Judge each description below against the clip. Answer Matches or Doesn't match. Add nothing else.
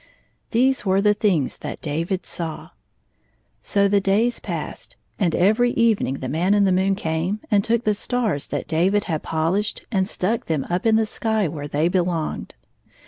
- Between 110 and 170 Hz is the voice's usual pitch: Doesn't match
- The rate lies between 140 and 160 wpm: Doesn't match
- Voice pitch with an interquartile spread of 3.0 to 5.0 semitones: Matches